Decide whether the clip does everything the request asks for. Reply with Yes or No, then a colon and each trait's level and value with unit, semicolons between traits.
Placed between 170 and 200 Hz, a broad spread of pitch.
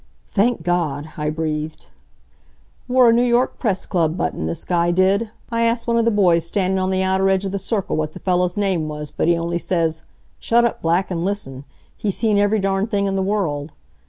No: high, 190 Hz; average, 3.7 semitones